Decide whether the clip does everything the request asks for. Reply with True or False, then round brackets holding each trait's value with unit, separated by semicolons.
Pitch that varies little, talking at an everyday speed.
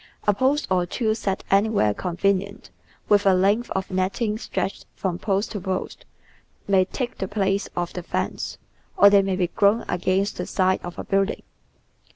True (1.8 semitones; 175 wpm)